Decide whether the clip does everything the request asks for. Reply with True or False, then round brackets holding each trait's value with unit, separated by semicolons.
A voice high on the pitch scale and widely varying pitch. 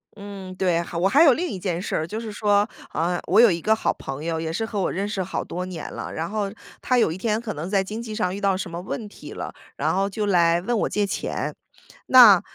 False (195 Hz; 3.5 semitones)